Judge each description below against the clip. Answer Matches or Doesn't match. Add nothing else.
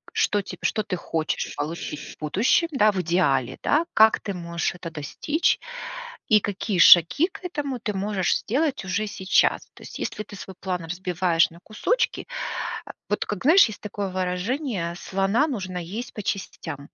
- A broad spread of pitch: Doesn't match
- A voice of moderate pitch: Doesn't match